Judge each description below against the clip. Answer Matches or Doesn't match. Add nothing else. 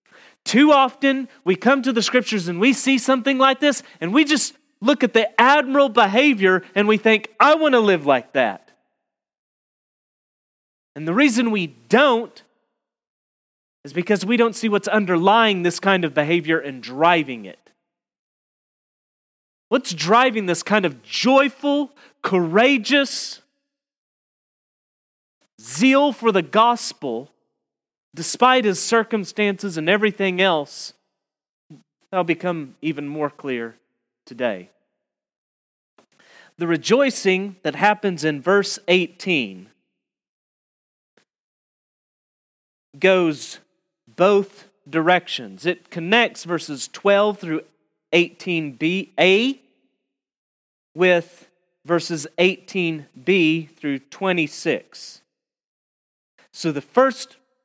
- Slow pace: Matches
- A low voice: Doesn't match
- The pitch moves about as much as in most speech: Doesn't match